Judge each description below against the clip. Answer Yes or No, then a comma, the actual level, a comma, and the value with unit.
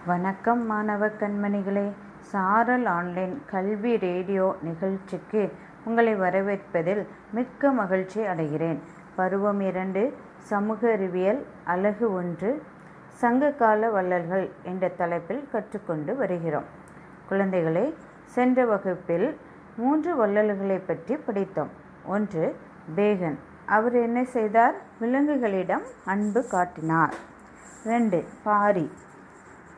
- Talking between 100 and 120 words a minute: No, average, 85 wpm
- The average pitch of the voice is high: Yes, high, 200 Hz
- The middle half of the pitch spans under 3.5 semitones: No, average, 3.8 semitones